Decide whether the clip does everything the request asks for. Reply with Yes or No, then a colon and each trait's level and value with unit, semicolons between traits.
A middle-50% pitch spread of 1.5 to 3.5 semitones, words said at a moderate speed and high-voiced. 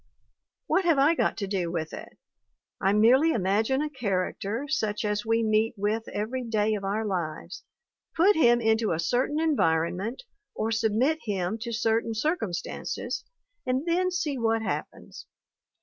No: average, 4.5 semitones; average, 150 wpm; high, 225 Hz